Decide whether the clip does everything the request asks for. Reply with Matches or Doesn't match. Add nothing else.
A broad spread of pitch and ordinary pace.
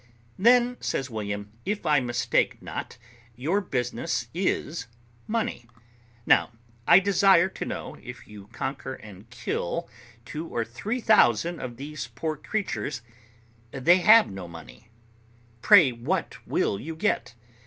Doesn't match